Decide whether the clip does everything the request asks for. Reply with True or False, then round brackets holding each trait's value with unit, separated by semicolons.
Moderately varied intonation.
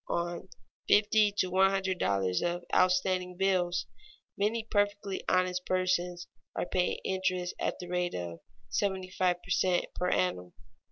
False (1.3 semitones)